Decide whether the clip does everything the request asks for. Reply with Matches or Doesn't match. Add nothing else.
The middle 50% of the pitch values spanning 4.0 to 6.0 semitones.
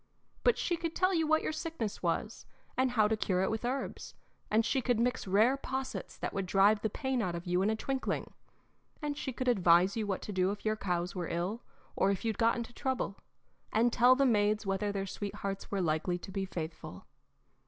Matches